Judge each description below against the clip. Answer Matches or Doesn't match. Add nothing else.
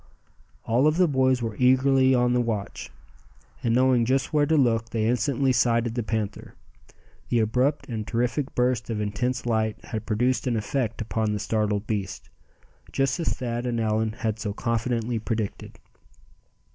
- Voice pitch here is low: Matches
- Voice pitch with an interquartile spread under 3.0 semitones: Matches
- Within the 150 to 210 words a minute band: Matches